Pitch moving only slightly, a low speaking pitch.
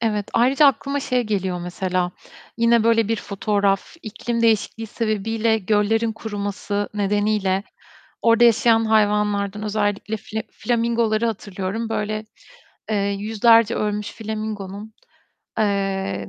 No: narrow, 2.0 semitones; high, 215 Hz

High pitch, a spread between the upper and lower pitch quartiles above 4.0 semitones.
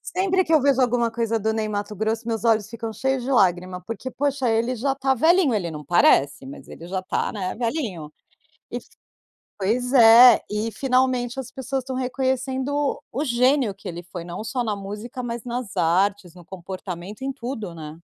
Yes: high, 230 Hz; average, 5.0 semitones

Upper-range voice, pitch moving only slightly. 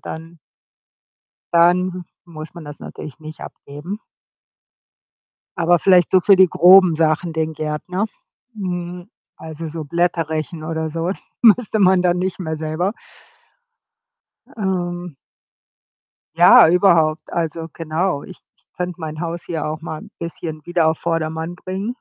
No: medium, 170 Hz; narrow, 2.3 semitones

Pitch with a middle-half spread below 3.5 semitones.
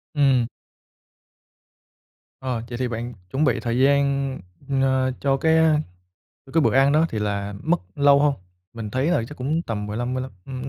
Yes: average, 3.1 semitones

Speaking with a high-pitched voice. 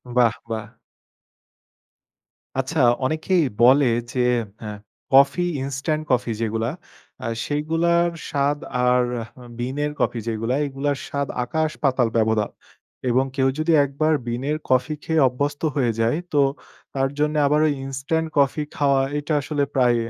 No: medium, 140 Hz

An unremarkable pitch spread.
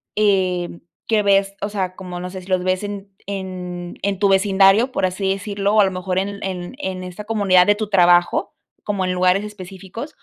No: narrow, 1.8 semitones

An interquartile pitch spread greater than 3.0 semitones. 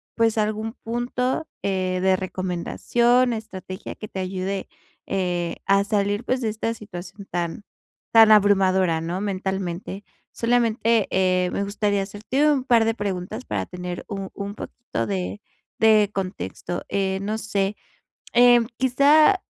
Yes: average, 3.4 semitones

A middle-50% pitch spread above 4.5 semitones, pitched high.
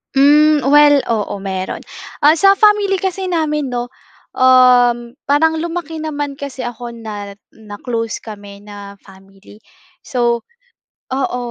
Yes: wide, 5.5 semitones; very high, 255 Hz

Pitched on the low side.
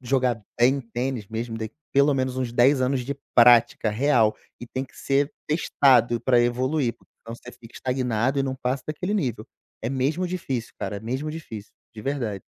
Yes: low, 125 Hz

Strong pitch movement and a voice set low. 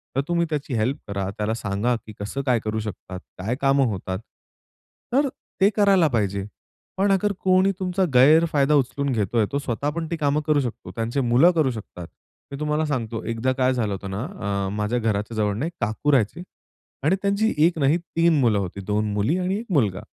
Yes: wide, 6.9 semitones; low, 130 Hz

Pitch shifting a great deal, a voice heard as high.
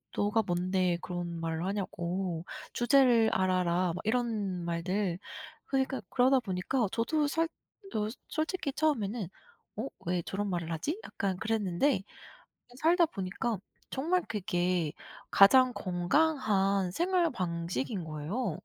Yes: wide, 6.2 semitones; high, 200 Hz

